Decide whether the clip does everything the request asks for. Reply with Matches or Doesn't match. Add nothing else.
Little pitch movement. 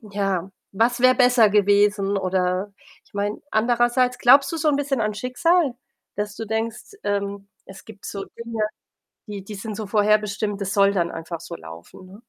Doesn't match